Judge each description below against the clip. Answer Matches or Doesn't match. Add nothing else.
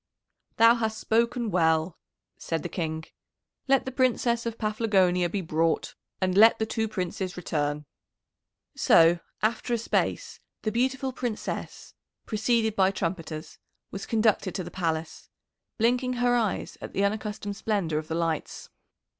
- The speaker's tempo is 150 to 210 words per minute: Doesn't match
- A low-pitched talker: Doesn't match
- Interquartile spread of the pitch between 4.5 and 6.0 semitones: Matches